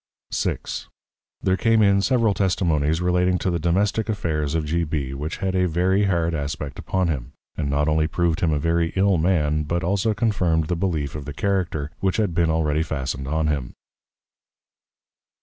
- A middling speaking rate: Yes, average, 180 wpm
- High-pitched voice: No, very low, 85 Hz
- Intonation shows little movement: No, average, 3.7 semitones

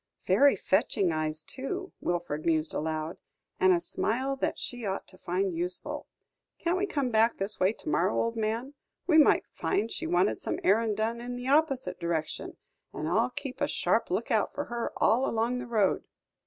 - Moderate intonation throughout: No, wide, 6.0 semitones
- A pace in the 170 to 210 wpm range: Yes, average, 185 wpm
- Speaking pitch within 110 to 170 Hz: No, high, 220 Hz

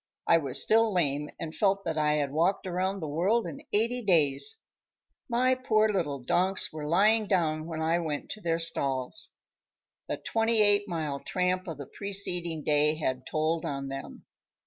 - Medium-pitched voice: Yes, medium, 170 Hz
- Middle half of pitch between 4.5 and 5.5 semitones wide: Yes, average, 5.0 semitones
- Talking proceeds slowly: No, average, 170 wpm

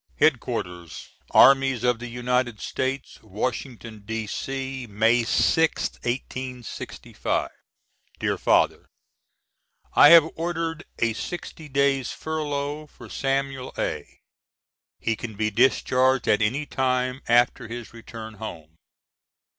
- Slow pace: Yes, slow, 110 wpm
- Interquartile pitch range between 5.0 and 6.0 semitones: No, average, 3.3 semitones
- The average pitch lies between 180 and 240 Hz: No, low, 125 Hz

